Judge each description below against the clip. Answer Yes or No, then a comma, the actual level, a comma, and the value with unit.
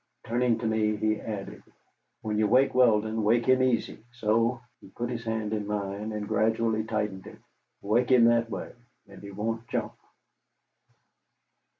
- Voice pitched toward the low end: Yes, low, 110 Hz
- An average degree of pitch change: No, narrow, 1.7 semitones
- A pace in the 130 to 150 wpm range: No, average, 160 wpm